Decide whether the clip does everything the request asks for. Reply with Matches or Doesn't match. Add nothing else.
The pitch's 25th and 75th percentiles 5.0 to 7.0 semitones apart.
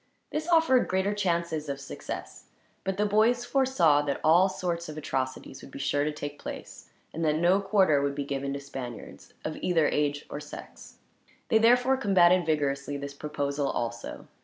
Matches